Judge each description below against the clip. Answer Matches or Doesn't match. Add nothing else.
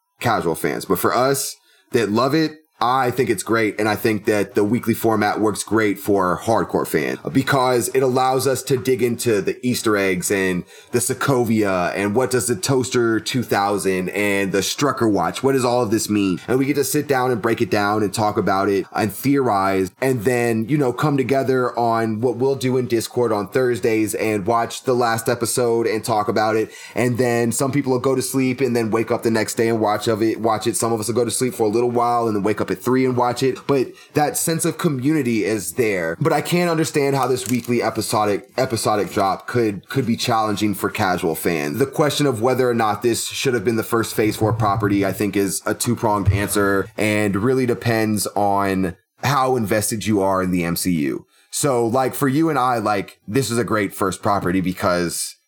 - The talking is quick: Matches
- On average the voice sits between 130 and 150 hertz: Doesn't match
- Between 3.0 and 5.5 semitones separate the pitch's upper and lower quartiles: Matches